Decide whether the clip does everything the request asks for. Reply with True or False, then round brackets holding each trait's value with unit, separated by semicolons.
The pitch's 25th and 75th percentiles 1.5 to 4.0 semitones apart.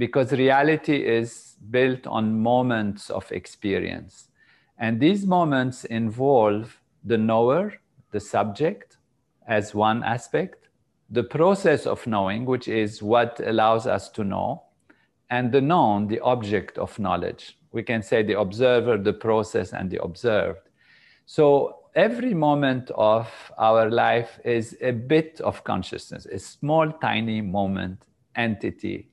True (3.3 semitones)